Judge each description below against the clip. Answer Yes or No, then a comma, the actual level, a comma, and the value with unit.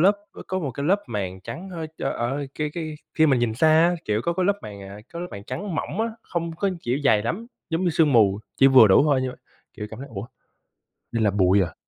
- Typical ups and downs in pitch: No, wide, 8.0 semitones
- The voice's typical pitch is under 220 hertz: Yes, medium, 140 Hz